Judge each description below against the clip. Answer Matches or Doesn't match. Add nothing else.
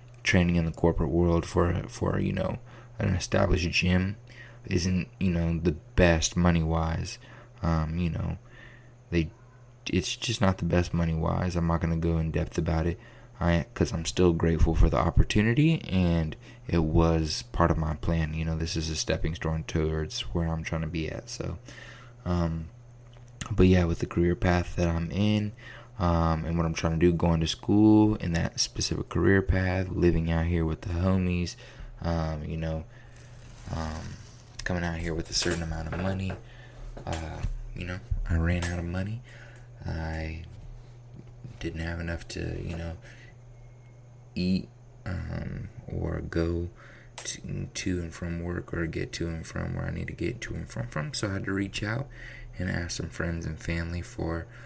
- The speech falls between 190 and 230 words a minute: Doesn't match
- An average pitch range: Doesn't match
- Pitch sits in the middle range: Doesn't match